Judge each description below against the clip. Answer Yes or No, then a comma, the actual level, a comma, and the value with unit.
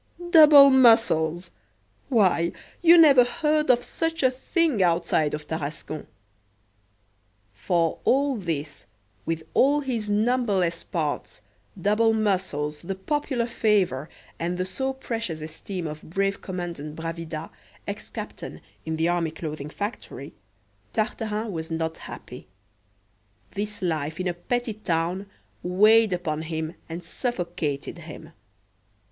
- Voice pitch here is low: No, medium, 185 Hz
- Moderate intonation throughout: No, wide, 6.1 semitones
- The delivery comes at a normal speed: No, slow, 120 wpm